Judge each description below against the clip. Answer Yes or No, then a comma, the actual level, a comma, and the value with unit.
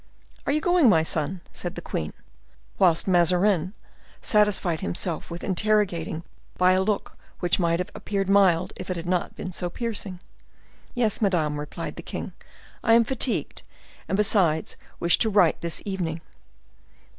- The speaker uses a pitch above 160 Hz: Yes, medium, 185 Hz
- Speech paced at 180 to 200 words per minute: No, average, 155 wpm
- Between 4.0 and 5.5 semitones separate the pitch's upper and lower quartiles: No, average, 3.6 semitones